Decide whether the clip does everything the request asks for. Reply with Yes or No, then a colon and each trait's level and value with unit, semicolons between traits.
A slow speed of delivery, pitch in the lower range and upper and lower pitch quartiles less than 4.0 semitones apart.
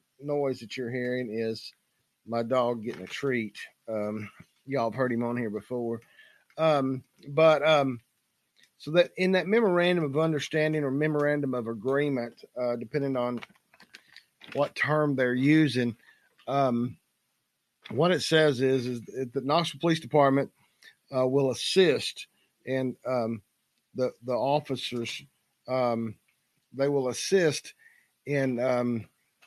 Yes: slow, 130 wpm; low, 130 Hz; average, 3.4 semitones